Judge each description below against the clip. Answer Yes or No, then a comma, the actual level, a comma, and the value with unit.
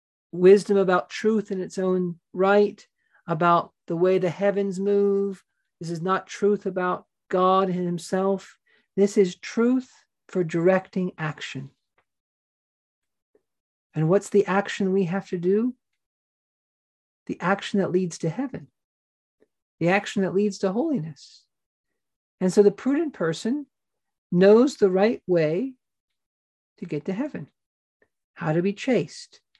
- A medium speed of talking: No, slow, 130 wpm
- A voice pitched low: No, high, 195 Hz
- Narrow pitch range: Yes, narrow, 2.2 semitones